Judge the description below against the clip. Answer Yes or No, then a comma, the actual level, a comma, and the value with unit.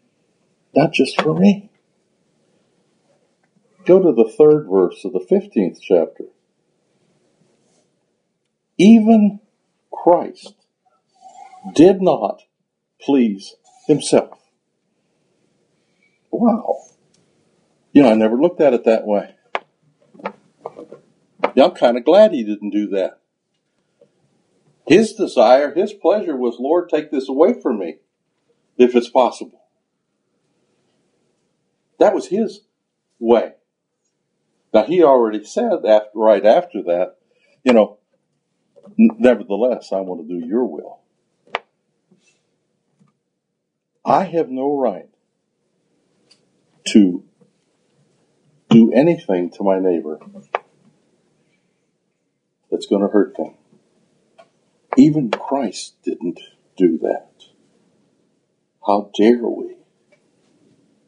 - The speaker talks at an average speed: No, slow, 95 wpm